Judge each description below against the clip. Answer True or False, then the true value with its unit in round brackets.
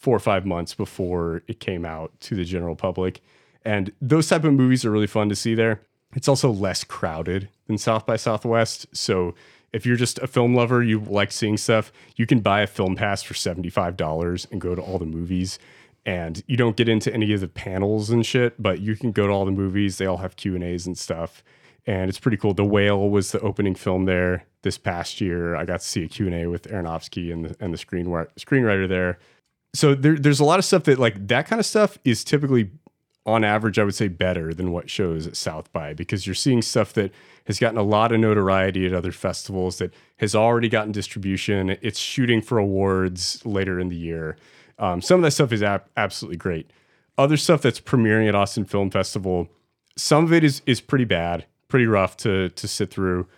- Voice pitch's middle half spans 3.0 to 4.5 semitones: True (4.1 semitones)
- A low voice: True (100 Hz)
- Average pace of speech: False (220 wpm)